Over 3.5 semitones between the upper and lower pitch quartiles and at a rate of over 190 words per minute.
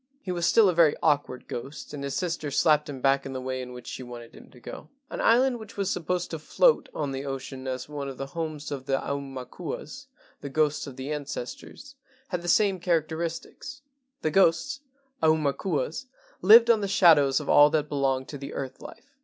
Yes: average, 4.6 semitones; fast, 205 wpm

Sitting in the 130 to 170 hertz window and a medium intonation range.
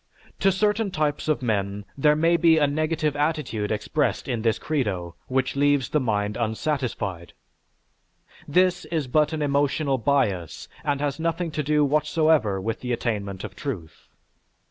No: medium, 140 Hz; wide, 5.8 semitones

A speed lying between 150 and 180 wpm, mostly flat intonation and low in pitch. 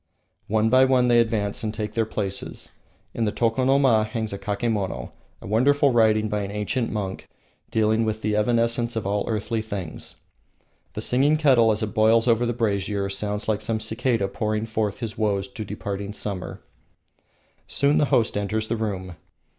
Yes: average, 170 wpm; narrow, 2.1 semitones; low, 110 Hz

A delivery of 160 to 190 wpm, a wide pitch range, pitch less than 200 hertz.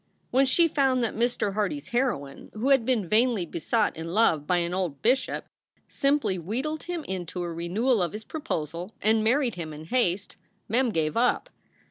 No: average, 180 wpm; wide, 6.9 semitones; high, 215 Hz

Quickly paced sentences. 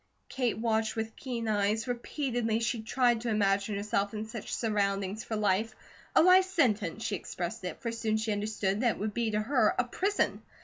No: average, 190 wpm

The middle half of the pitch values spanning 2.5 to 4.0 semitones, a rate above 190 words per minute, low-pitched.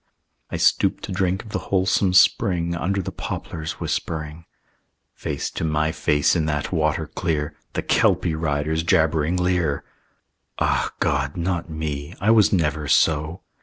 No: average, 3.0 semitones; average, 145 wpm; very low, 80 Hz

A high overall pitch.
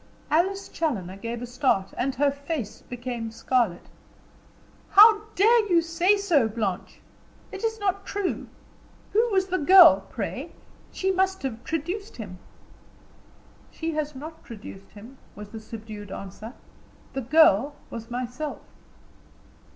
Yes: very high, 280 Hz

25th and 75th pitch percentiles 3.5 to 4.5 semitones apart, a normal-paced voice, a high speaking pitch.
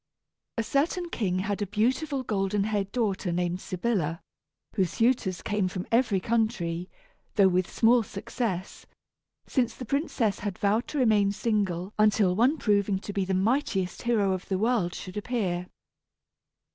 Yes: average, 3.8 semitones; average, 150 wpm; high, 205 Hz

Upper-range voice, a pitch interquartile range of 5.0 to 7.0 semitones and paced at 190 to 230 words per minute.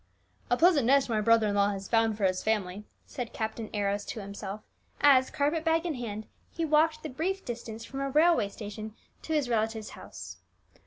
Yes: high, 230 Hz; wide, 5.5 semitones; average, 195 wpm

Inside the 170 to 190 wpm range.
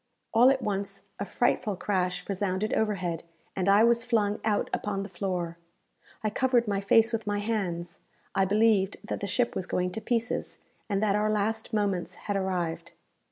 Yes: average, 175 wpm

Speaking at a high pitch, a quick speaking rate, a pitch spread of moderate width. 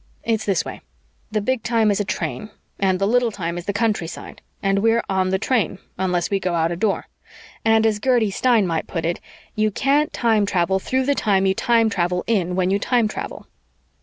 Yes: high, 205 Hz; fast, 210 wpm; average, 3.4 semitones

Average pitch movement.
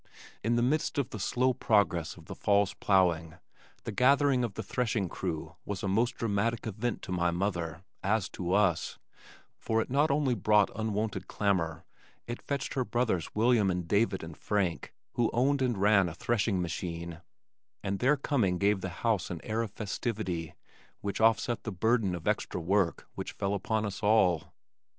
Yes: average, 4.4 semitones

